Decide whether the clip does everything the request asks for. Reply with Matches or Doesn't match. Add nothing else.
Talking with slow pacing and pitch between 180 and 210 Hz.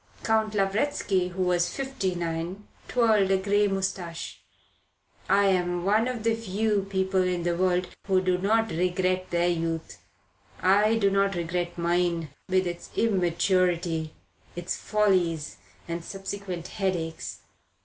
Matches